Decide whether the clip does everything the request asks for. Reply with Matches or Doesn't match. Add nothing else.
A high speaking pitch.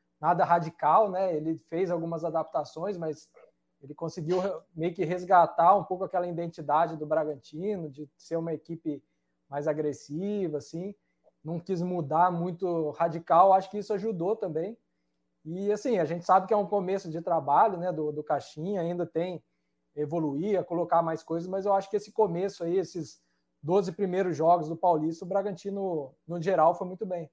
Doesn't match